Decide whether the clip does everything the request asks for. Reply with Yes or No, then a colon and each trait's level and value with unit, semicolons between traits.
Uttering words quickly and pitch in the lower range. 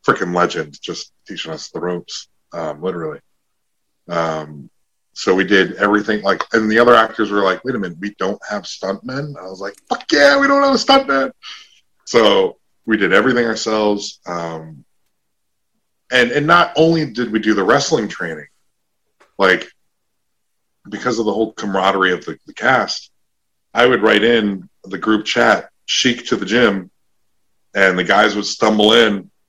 No: average, 165 wpm; low, 110 Hz